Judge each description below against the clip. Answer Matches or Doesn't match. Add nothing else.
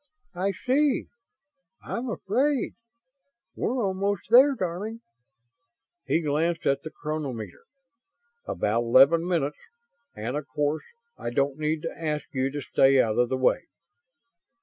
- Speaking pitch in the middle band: Matches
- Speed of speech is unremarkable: Doesn't match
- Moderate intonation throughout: Doesn't match